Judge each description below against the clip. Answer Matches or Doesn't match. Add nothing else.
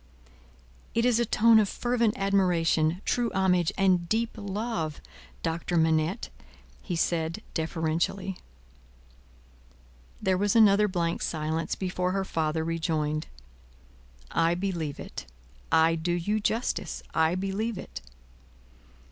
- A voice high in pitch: Doesn't match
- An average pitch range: Matches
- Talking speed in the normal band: Doesn't match